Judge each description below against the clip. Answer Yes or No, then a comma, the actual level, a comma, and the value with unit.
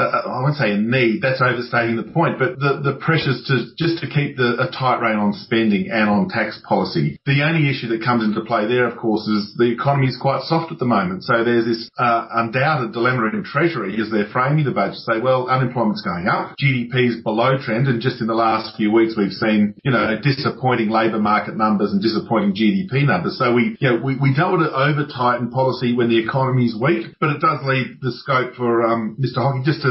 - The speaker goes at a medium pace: No, fast, 235 wpm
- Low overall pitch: Yes, low, 125 Hz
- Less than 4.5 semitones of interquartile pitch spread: Yes, average, 3.3 semitones